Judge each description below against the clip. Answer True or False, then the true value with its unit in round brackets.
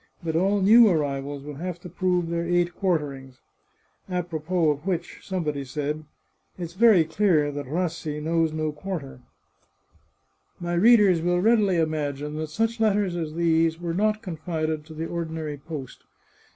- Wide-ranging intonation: False (3.1 semitones)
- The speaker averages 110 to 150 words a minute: False (165 wpm)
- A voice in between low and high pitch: True (165 Hz)